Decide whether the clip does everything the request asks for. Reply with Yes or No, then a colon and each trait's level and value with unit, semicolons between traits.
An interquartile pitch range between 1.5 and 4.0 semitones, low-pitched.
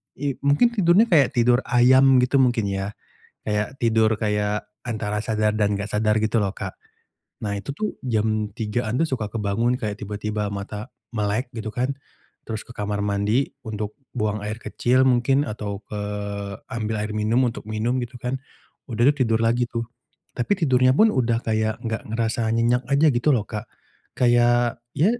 Yes: average, 2.8 semitones; low, 115 Hz